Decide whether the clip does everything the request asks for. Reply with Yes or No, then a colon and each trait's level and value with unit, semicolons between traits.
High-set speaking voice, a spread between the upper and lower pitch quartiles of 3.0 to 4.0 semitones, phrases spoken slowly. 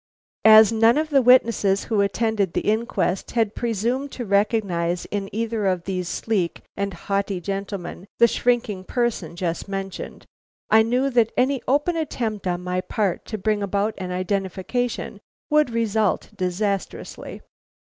No: high, 210 Hz; average, 3.5 semitones; average, 145 wpm